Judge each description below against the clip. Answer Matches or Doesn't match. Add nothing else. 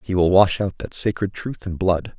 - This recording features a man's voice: Matches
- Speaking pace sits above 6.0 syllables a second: Doesn't match